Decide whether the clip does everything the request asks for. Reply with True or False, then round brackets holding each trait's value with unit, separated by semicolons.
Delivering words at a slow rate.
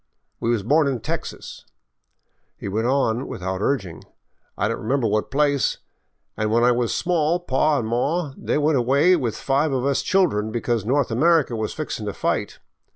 False (180 wpm)